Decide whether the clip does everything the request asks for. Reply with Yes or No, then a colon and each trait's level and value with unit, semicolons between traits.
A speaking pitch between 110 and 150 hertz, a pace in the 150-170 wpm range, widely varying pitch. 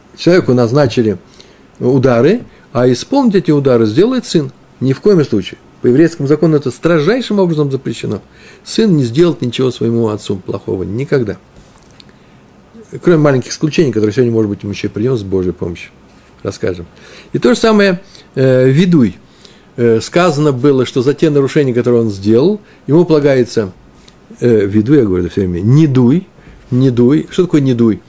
Yes: low, 135 Hz; fast, 160 wpm; wide, 6.2 semitones